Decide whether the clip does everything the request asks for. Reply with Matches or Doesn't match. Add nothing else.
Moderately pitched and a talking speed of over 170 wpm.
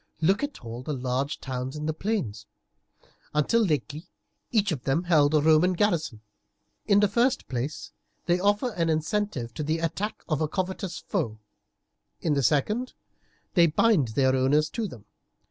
Doesn't match